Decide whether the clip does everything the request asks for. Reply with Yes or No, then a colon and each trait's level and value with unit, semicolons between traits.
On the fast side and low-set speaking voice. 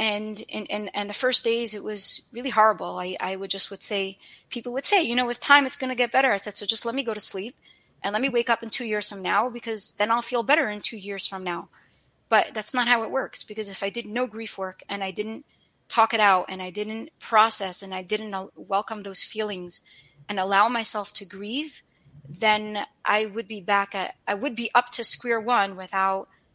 No: fast, 235 wpm; high, 215 Hz